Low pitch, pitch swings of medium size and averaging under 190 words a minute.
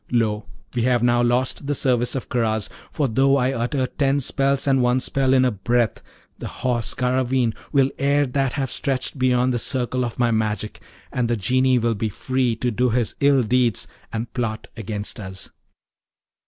No: low, 125 Hz; narrow, 2.2 semitones; average, 180 wpm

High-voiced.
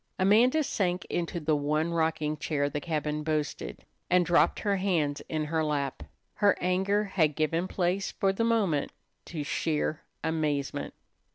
No: medium, 160 Hz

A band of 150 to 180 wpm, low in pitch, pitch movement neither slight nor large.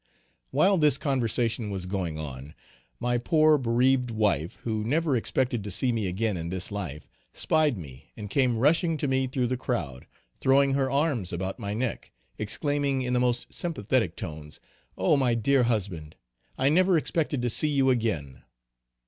No: average, 165 wpm; low, 120 Hz; wide, 5.8 semitones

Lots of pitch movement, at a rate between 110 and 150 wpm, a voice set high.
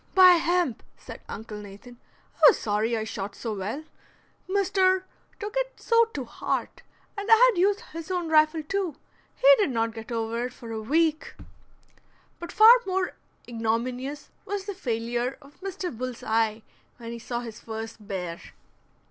No: wide, 8.7 semitones; average, 165 wpm; very high, 255 Hz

